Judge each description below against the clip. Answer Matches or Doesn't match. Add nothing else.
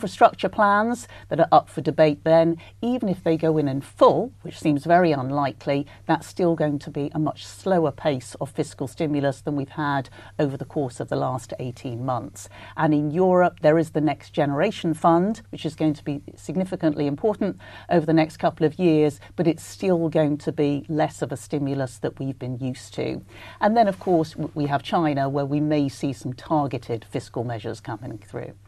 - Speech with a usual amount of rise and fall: Matches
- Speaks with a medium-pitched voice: Matches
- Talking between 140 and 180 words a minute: Doesn't match